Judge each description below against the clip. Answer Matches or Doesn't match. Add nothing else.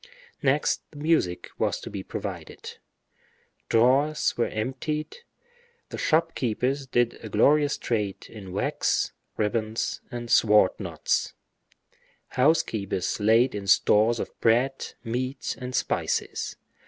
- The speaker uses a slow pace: Matches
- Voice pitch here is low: Matches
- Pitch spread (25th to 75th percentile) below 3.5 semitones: Doesn't match